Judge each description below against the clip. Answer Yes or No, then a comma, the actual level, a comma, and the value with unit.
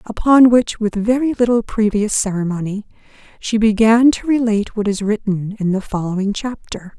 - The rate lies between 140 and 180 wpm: Yes, average, 155 wpm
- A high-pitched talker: Yes, high, 215 Hz